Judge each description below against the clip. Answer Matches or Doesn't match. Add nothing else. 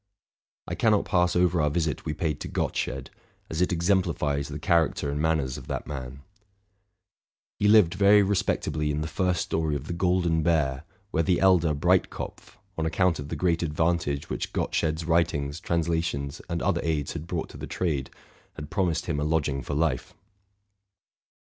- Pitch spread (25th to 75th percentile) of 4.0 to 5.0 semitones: Doesn't match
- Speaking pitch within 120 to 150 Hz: Doesn't match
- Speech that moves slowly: Doesn't match